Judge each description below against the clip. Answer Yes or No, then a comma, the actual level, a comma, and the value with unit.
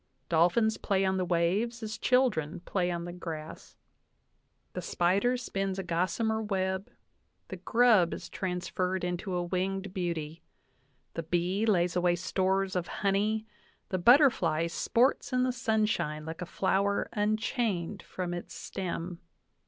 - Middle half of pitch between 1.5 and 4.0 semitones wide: Yes, average, 3.6 semitones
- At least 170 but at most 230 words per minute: No, slow, 135 wpm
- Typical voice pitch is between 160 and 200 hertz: Yes, high, 190 Hz